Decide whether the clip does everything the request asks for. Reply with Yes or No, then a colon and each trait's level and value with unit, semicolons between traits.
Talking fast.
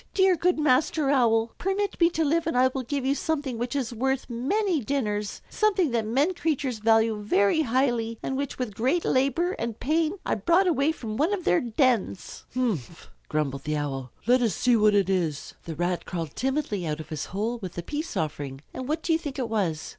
Yes: fast, 210 wpm